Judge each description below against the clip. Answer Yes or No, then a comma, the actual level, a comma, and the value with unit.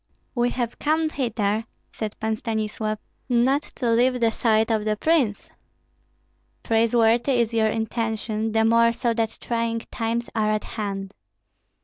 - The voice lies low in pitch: No, high, 225 Hz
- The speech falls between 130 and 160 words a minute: Yes, average, 140 wpm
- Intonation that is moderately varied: No, narrow, 1.6 semitones